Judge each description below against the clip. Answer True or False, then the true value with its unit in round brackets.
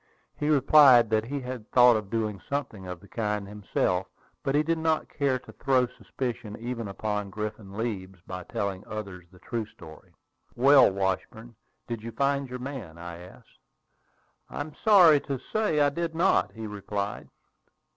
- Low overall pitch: True (115 Hz)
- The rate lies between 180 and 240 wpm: False (165 wpm)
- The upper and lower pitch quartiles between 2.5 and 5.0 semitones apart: False (5.5 semitones)